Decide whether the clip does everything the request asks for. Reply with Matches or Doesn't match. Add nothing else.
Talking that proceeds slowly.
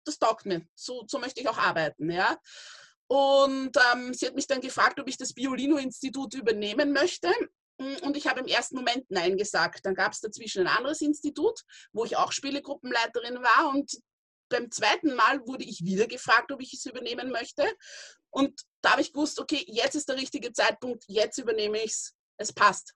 Doesn't match